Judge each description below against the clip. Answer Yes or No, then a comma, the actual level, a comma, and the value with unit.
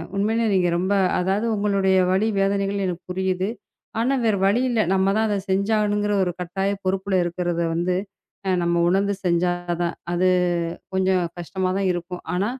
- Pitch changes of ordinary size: No, narrow, 2.1 semitones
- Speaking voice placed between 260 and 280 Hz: No, high, 190 Hz